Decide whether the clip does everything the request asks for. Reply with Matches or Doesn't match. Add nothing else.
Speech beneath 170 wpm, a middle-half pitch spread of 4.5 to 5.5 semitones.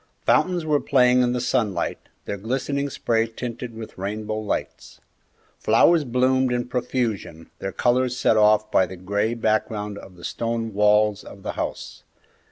Doesn't match